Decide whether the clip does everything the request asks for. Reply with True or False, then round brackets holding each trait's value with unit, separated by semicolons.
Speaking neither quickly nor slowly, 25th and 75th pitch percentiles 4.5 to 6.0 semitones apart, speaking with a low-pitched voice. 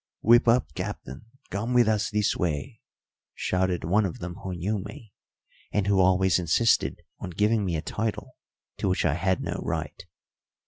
False (170 wpm; 3.3 semitones; 95 Hz)